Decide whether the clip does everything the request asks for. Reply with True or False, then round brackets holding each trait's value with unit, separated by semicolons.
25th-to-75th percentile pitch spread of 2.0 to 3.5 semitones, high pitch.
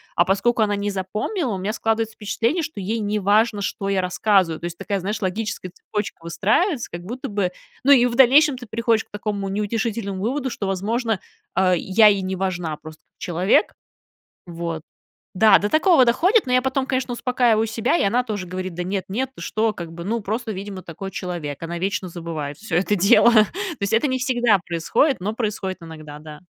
False (4.1 semitones; 205 Hz)